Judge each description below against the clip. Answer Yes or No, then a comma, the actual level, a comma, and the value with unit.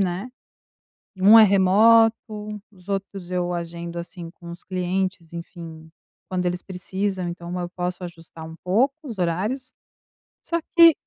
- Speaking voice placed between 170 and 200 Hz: Yes, medium, 185 Hz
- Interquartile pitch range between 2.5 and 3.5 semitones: Yes, average, 3.1 semitones